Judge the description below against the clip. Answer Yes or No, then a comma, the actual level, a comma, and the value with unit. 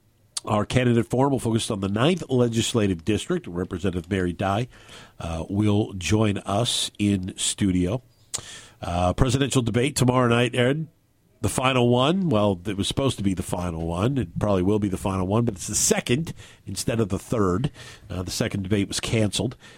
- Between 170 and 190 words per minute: Yes, average, 175 wpm